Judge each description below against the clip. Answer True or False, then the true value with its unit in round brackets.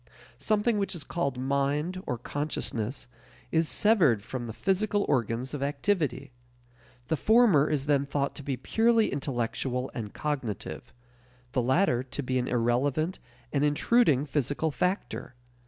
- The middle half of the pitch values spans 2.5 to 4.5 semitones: False (5.1 semitones)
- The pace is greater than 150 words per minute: False (140 wpm)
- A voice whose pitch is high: False (140 Hz)